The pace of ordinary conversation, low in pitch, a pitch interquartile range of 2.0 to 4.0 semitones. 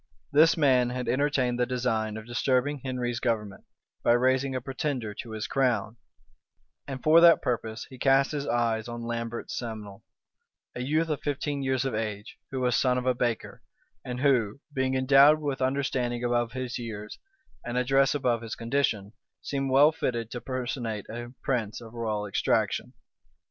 Yes: average, 165 wpm; low, 125 Hz; average, 2.7 semitones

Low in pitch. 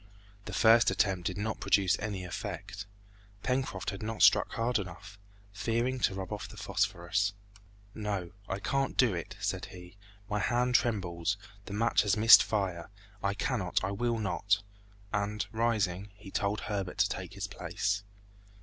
Yes: low, 100 Hz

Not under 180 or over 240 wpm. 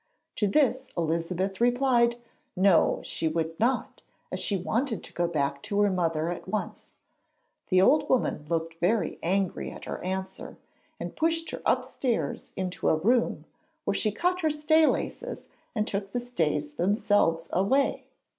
No: average, 155 wpm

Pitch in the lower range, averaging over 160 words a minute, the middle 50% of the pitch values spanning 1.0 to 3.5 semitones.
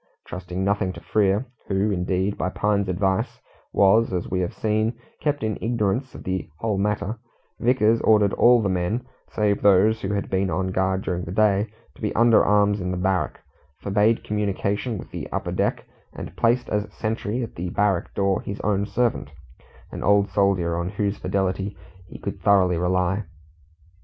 Yes: low, 100 Hz; average, 175 wpm; narrow, 2.4 semitones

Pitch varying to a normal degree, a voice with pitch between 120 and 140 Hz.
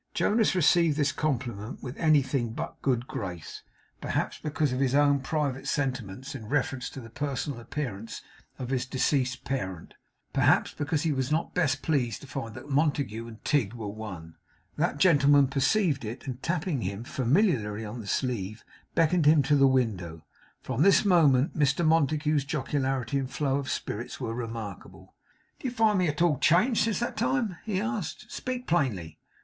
Yes: average, 4.7 semitones; low, 135 Hz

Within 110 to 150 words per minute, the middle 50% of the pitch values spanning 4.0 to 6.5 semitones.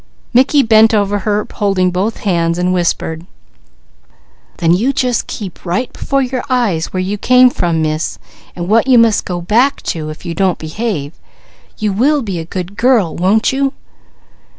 No: average, 170 wpm; average, 5.3 semitones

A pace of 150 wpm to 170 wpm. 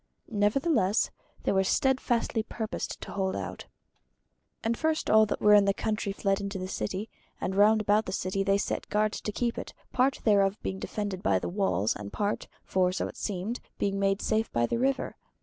No: average, 190 wpm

